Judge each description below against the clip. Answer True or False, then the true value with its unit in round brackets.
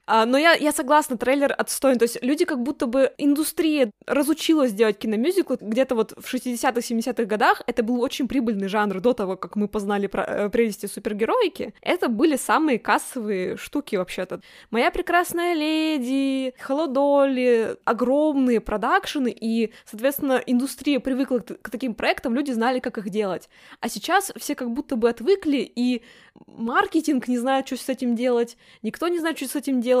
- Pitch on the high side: True (255 Hz)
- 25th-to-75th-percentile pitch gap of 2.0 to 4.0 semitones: True (3.7 semitones)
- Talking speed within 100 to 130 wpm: False (160 wpm)